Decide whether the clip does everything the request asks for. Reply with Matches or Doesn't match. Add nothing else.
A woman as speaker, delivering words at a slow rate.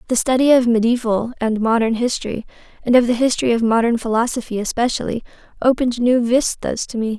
Doesn't match